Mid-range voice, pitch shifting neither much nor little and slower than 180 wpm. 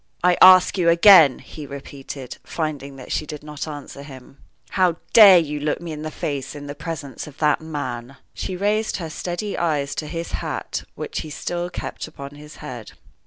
No: medium, 150 Hz; average, 3.4 semitones; average, 190 wpm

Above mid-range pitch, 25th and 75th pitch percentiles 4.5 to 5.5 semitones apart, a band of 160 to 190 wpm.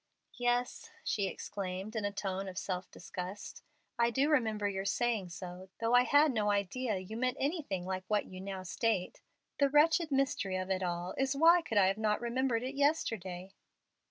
Yes: high, 210 Hz; average, 5.2 semitones; average, 185 wpm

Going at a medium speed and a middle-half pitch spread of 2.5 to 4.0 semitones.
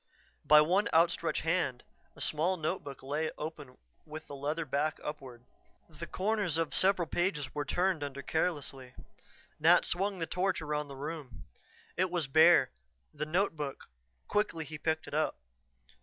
Yes: average, 150 wpm; average, 3.3 semitones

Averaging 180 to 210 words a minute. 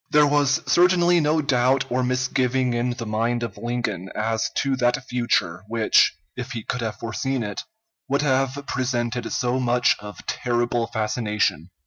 No: average, 155 wpm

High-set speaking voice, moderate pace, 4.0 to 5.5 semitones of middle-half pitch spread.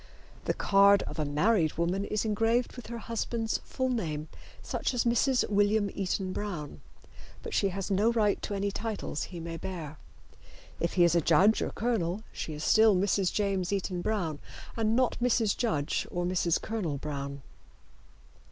Yes: high, 200 Hz; average, 170 wpm; average, 4.6 semitones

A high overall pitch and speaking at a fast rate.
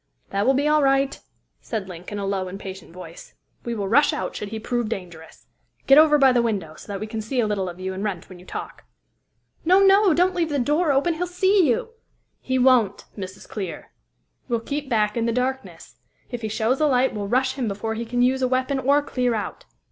Yes: high, 240 Hz; fast, 230 wpm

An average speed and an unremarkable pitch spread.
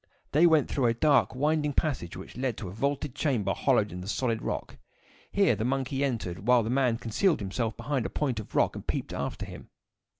No: fast, 210 wpm; average, 4.3 semitones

